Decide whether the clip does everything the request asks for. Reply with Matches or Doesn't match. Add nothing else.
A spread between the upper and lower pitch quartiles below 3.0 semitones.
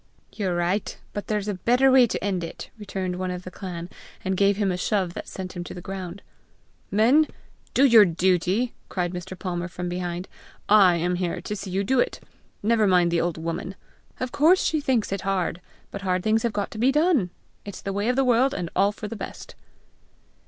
Doesn't match